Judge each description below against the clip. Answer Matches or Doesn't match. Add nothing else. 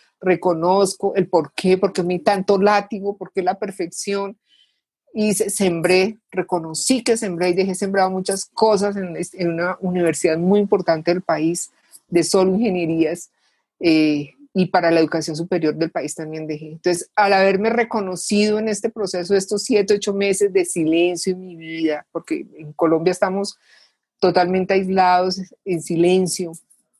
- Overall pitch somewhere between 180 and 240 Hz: Matches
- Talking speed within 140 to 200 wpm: Matches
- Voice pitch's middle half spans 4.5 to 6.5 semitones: Doesn't match